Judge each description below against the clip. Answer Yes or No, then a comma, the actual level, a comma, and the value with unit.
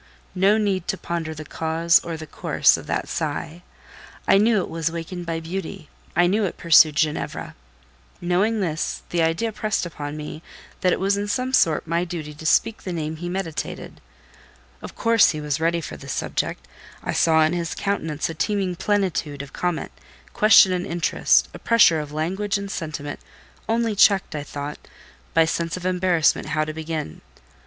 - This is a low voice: No, medium, 170 Hz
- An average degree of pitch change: Yes, average, 3.5 semitones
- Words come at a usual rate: Yes, average, 180 wpm